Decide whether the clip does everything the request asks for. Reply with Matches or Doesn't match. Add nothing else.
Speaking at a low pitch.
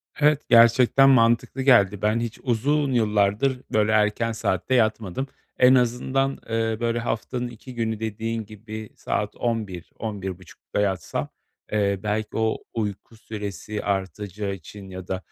Matches